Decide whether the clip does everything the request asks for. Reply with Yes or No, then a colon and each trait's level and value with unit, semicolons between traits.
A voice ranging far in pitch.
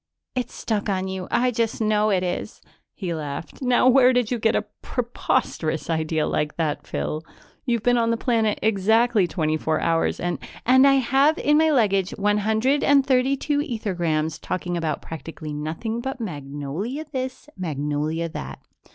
Yes: wide, 7.4 semitones